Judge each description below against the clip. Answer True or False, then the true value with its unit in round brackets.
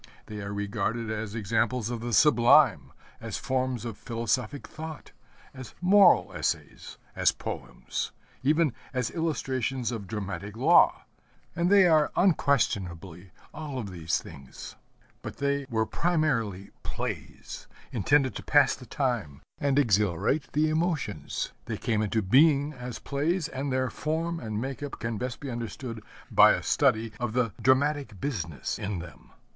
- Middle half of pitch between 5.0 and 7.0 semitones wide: True (5.3 semitones)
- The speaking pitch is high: False (125 Hz)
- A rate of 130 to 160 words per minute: True (145 wpm)